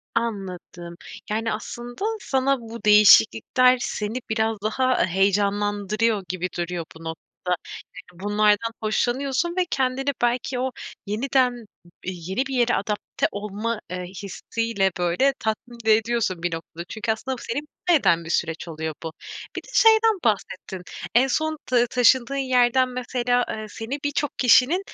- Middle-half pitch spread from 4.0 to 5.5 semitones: Yes, average, 4.7 semitones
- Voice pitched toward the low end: No, high, 225 Hz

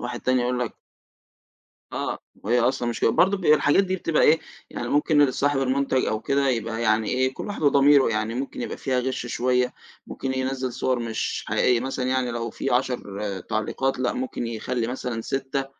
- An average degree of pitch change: No, narrow, 2.2 semitones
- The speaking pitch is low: Yes, low, 130 Hz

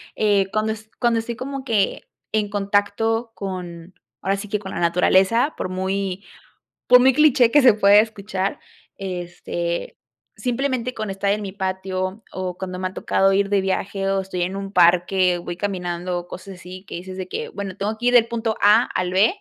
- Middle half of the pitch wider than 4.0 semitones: No, average, 2.9 semitones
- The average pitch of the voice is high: Yes, high, 195 Hz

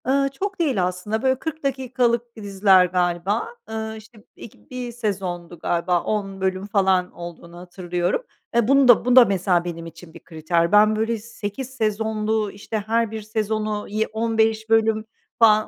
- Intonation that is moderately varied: Yes, average, 4.0 semitones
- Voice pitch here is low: No, high, 215 Hz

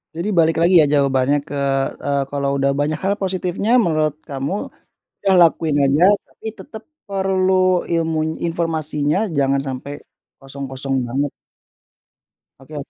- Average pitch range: Yes, average, 3.4 semitones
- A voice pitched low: No, medium, 150 Hz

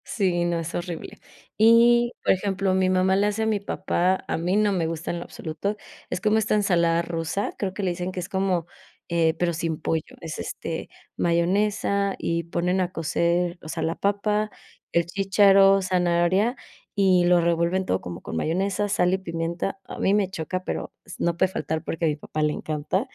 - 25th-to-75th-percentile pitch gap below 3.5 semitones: Yes, average, 2.8 semitones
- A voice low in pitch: No, medium, 180 Hz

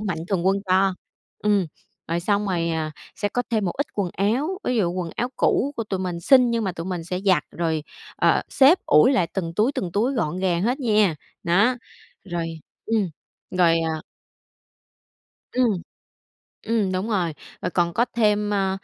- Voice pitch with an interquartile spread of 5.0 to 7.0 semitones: No, average, 4.5 semitones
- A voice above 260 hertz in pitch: No, high, 190 Hz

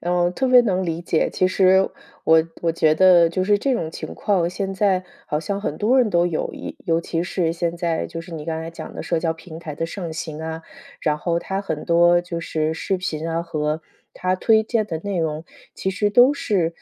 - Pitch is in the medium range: Yes, medium, 170 Hz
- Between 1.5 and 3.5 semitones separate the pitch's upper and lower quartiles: Yes, average, 2.8 semitones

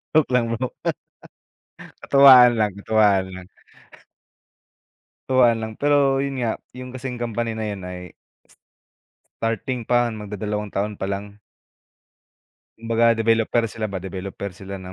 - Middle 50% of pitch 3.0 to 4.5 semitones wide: Yes, average, 3.5 semitones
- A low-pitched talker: Yes, low, 110 Hz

